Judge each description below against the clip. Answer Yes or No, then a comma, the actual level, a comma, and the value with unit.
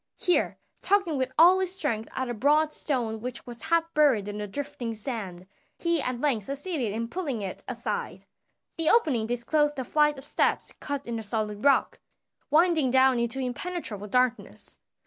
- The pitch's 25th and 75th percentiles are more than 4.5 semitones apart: Yes, average, 5.0 semitones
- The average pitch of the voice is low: No, very high, 260 Hz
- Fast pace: No, average, 170 wpm